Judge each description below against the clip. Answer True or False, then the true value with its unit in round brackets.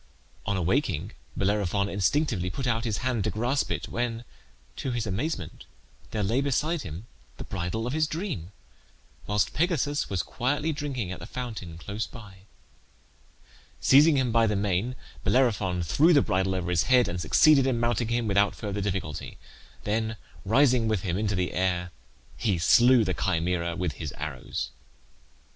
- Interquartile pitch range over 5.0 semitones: True (5.5 semitones)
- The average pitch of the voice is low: True (110 Hz)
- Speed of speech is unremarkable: True (160 wpm)